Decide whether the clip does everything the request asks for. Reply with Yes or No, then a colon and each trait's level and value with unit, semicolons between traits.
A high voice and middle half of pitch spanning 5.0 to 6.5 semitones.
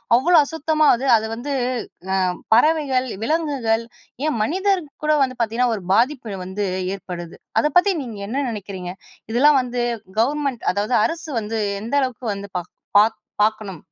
Yes: high, 245 Hz; wide, 5.6 semitones